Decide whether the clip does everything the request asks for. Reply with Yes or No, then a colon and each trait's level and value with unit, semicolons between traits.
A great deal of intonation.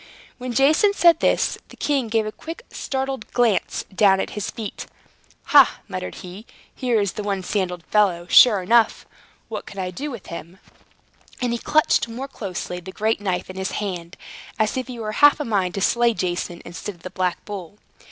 No: average, 4.7 semitones